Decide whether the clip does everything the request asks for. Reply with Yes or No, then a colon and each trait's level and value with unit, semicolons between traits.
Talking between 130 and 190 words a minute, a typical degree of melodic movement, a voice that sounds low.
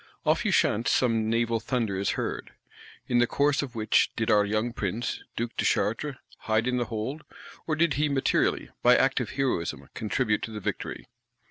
Yes: average, 175 wpm; average, 3.3 semitones; low, 115 Hz